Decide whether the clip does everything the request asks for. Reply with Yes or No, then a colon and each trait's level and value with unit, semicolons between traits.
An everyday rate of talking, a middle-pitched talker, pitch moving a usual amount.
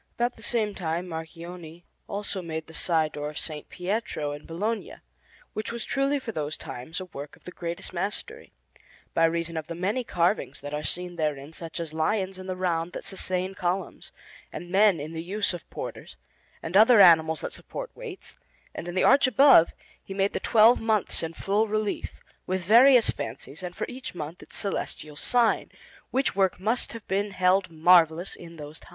Yes: average, 190 wpm; medium, 180 Hz; average, 4.5 semitones